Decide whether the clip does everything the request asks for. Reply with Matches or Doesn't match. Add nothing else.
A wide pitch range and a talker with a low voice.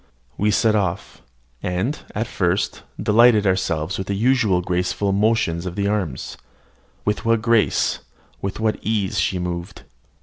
Doesn't match